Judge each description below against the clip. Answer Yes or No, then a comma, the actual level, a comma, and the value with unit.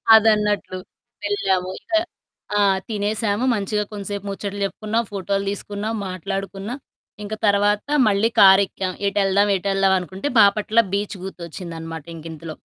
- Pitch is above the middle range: Yes, high, 200 Hz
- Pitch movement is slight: Yes, narrow, 1.5 semitones